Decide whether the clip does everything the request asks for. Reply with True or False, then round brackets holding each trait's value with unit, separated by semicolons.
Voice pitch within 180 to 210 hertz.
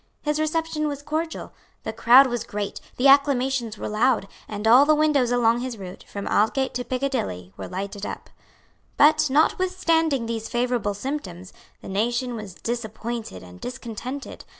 False (245 Hz)